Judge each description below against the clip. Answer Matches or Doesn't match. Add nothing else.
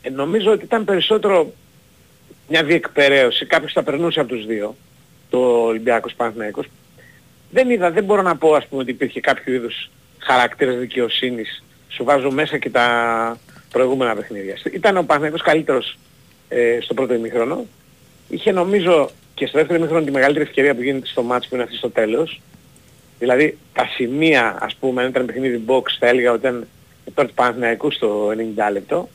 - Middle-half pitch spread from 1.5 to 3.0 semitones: Doesn't match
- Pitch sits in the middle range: Doesn't match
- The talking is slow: Doesn't match